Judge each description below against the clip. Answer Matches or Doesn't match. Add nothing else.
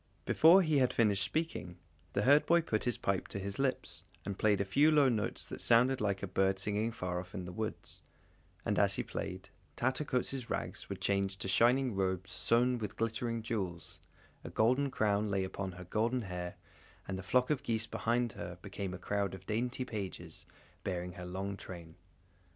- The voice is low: Matches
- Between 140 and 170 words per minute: Doesn't match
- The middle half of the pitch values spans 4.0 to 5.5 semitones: Matches